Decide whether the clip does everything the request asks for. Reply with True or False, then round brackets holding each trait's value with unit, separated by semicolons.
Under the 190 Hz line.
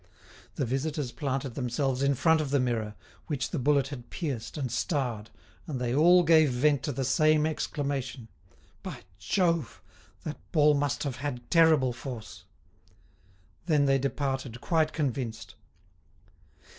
True (140 Hz)